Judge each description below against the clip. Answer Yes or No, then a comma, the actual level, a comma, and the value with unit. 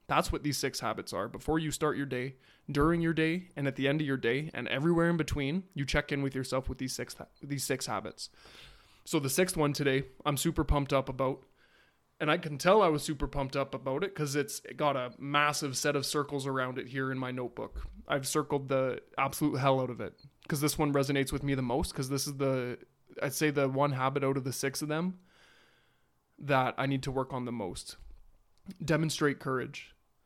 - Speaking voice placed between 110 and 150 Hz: Yes, medium, 140 Hz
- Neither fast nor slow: No, fast, 225 wpm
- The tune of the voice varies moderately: No, narrow, 2.2 semitones